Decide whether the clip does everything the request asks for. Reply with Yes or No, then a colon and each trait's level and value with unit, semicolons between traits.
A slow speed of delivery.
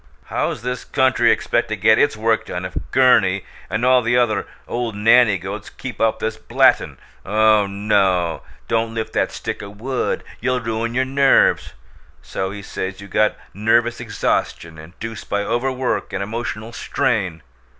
No: average, 160 wpm